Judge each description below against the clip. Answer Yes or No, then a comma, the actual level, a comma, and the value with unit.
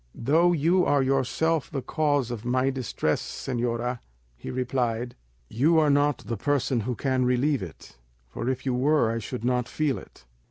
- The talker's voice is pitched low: Yes, low, 130 Hz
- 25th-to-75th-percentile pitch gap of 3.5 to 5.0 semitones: No, average, 3.1 semitones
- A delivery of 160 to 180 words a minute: Yes, average, 170 wpm